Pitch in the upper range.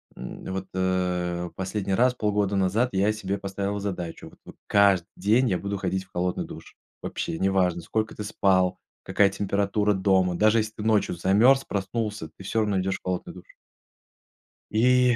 No: low, 100 Hz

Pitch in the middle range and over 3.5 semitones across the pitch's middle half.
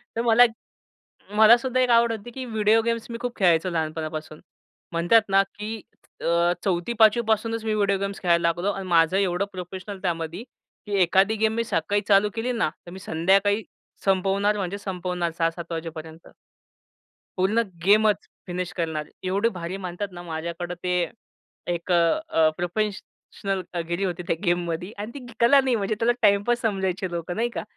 No: high, 195 Hz; average, 4.0 semitones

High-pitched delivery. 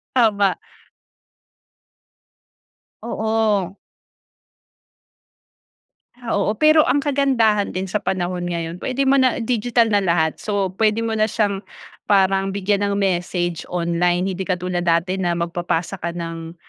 Yes: high, 195 Hz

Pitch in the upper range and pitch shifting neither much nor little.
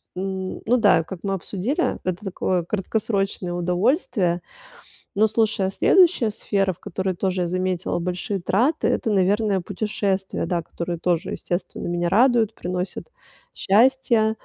Yes: high, 195 Hz; average, 3.3 semitones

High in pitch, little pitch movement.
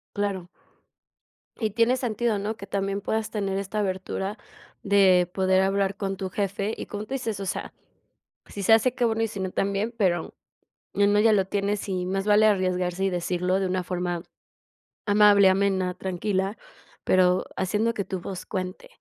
Yes: high, 195 Hz; narrow, 1.9 semitones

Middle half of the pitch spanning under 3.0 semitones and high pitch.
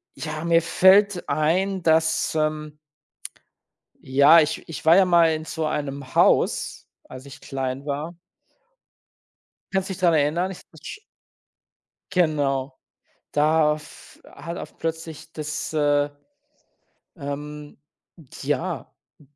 No: narrow, 2.5 semitones; medium, 155 Hz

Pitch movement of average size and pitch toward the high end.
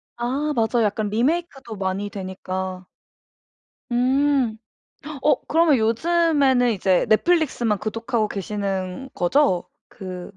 No: wide, 5.9 semitones; high, 225 Hz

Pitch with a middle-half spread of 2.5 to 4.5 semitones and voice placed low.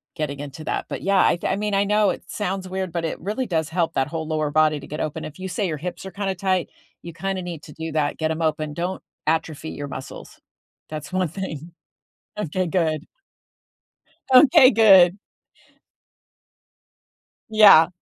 No: average, 3.6 semitones; medium, 170 Hz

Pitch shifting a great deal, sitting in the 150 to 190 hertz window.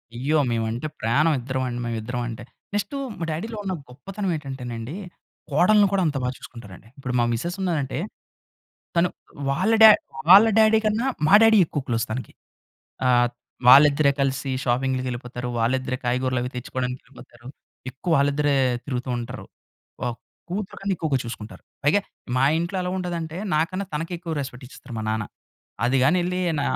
No: wide, 5.8 semitones; low, 135 Hz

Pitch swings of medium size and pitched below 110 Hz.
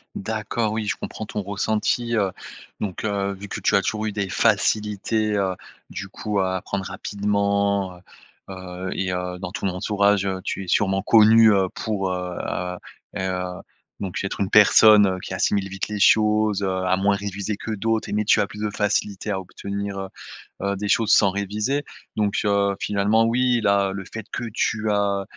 No: narrow, 1.8 semitones; low, 100 Hz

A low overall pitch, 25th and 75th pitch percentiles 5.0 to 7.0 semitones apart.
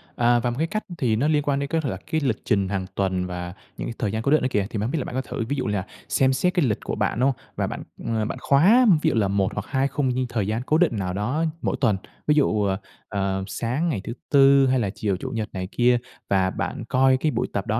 Yes: low, 120 Hz; wide, 5.5 semitones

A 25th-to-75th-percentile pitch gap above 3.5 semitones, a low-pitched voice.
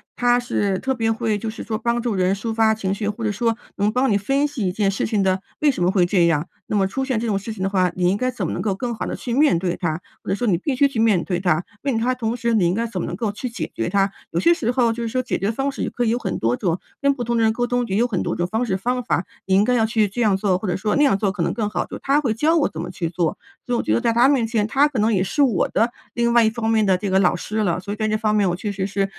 No: average, 3.9 semitones; high, 215 Hz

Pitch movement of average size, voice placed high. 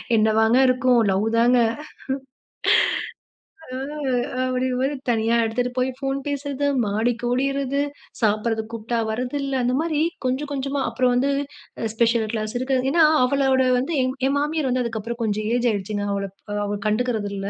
Yes: average, 3.4 semitones; very high, 250 Hz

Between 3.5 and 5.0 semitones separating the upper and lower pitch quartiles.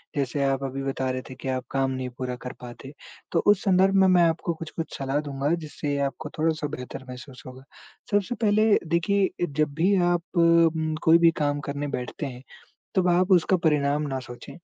Yes: average, 4.0 semitones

